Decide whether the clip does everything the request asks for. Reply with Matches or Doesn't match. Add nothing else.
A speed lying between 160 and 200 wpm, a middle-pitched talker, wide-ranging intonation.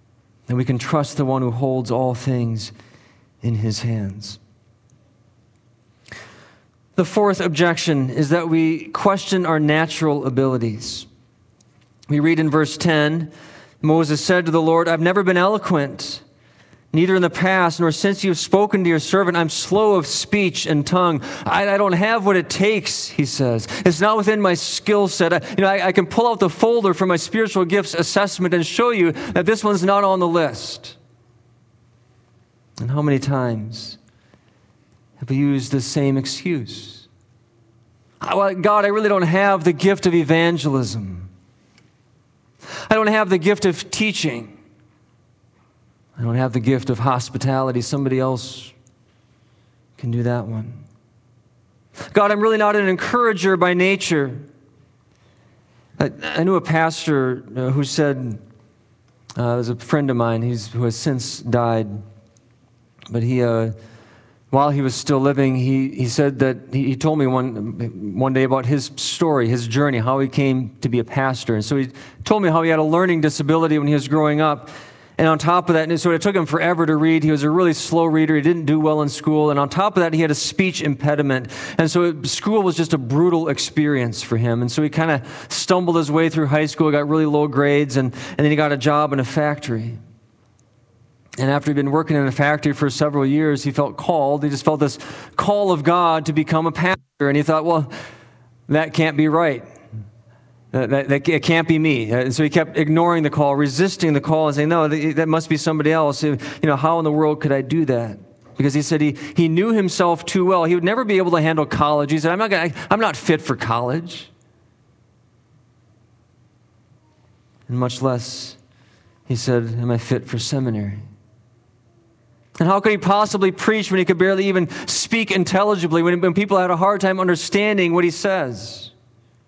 Matches